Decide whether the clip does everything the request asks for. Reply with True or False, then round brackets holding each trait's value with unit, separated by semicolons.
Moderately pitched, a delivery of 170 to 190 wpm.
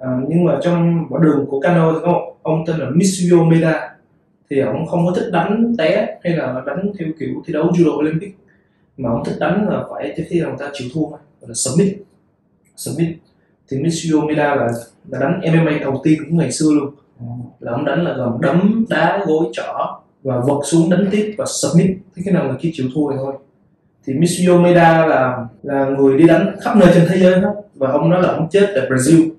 False (165 Hz; 215 wpm)